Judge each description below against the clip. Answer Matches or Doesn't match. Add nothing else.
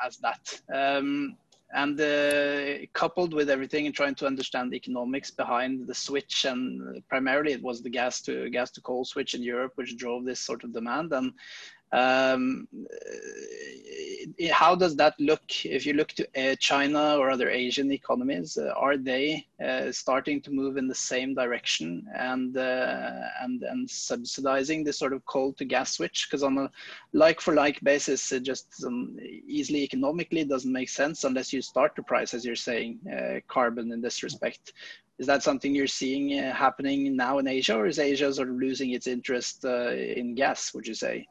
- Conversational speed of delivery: Matches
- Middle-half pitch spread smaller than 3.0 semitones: Matches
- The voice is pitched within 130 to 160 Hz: Matches